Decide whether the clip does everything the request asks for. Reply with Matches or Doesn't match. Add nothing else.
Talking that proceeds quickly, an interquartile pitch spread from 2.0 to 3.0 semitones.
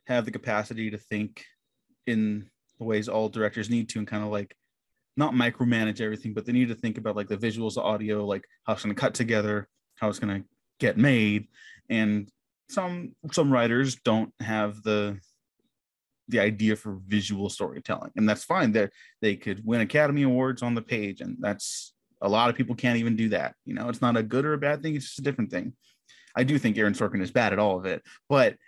Matches